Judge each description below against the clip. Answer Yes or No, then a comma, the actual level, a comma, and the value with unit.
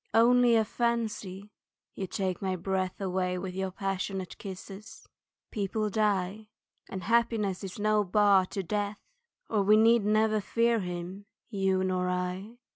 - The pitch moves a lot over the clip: No, narrow, 2.4 semitones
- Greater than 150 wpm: No, slow, 135 wpm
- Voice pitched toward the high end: Yes, high, 195 Hz